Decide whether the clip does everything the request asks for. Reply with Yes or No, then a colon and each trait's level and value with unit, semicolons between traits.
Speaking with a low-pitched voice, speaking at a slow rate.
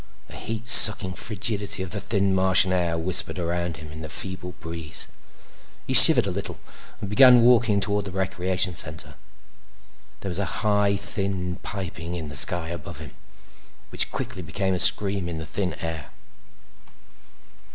No: very low, 95 Hz; average, 160 wpm